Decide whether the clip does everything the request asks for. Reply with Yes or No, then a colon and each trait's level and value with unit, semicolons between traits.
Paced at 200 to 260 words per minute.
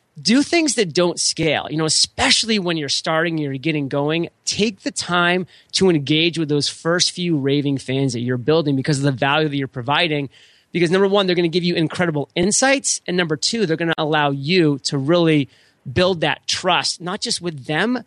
Yes: fast, 205 wpm